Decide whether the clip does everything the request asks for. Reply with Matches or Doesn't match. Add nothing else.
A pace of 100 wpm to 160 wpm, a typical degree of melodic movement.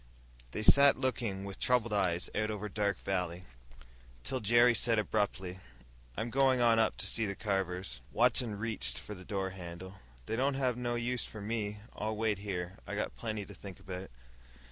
Doesn't match